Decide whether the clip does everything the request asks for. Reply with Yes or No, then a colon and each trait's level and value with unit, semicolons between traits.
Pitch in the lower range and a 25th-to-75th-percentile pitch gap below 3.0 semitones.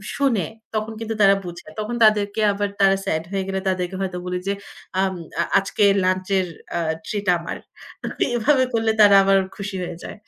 No: high, 200 Hz; narrow, 2.4 semitones